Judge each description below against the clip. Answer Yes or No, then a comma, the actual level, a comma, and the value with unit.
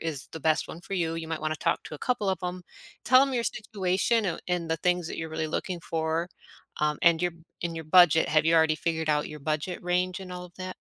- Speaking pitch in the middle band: Yes, medium, 170 Hz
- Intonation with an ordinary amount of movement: No, narrow, 2.3 semitones